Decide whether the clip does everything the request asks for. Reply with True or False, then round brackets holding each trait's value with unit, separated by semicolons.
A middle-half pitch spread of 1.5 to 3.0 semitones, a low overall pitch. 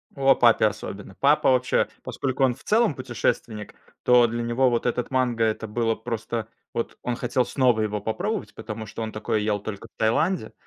True (2.7 semitones; 120 Hz)